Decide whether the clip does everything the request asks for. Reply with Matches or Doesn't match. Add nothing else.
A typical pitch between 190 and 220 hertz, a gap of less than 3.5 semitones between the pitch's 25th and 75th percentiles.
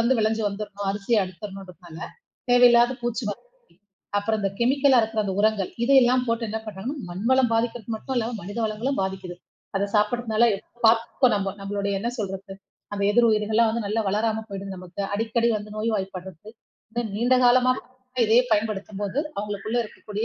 Matches